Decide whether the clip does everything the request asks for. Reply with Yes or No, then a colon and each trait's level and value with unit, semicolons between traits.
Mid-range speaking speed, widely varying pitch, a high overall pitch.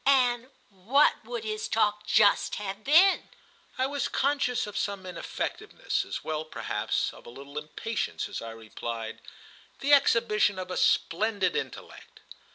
Yes: average, 150 wpm; wide, 6.9 semitones; high, 210 Hz